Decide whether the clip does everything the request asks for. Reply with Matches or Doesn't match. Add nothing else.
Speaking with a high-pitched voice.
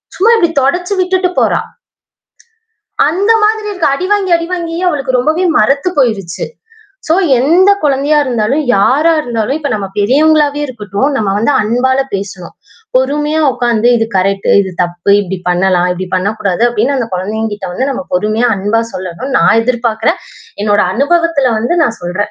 Matches